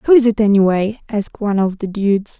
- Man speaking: No, female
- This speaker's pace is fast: Yes, fast, 225 wpm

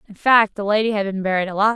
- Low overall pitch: No, high, 205 Hz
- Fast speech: Yes, fast, 275 wpm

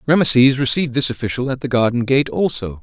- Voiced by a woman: No, male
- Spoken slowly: No, average, 190 wpm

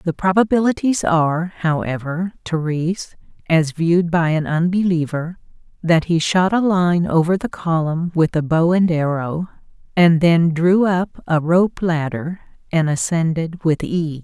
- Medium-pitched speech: Yes, medium, 170 Hz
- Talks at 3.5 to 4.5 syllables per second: Yes, 4.3 syllables/s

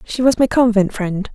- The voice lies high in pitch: Yes, high, 215 Hz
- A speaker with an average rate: No, fast, 225 wpm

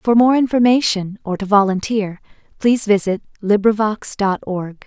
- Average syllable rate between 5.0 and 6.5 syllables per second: No, 4.8 syllables/s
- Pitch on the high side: Yes, high, 210 Hz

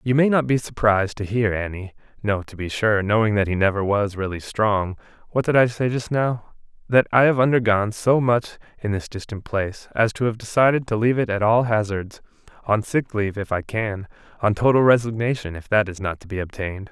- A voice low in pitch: Yes, low, 110 Hz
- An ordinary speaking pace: No, fast, 210 wpm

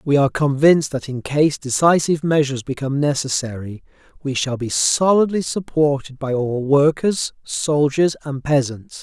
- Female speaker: No, male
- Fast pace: No, average, 140 wpm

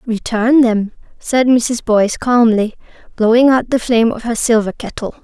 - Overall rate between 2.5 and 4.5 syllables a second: No, 4.9 syllables/s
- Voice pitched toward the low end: No, high, 230 Hz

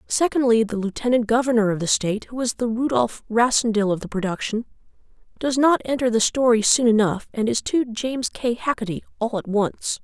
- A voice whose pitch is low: No, high, 230 Hz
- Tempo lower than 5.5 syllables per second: No, 5.6 syllables/s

